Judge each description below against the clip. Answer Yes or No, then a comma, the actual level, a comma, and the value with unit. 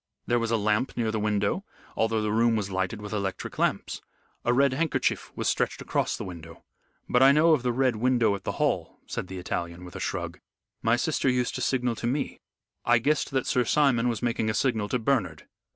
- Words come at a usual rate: No, fast, 215 wpm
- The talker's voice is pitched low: Yes, low, 115 Hz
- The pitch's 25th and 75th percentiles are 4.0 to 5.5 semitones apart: No, average, 3.5 semitones